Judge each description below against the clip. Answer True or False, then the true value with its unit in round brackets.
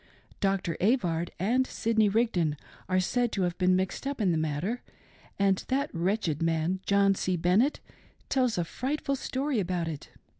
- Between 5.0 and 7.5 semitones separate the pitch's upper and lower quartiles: True (5.5 semitones)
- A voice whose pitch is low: False (195 Hz)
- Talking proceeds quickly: False (160 wpm)